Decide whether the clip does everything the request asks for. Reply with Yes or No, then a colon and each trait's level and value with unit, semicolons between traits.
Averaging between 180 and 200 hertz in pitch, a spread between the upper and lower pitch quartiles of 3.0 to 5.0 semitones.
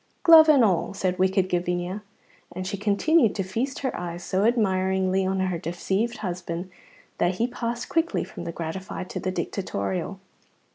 Yes: high, 190 Hz; average, 4.0 semitones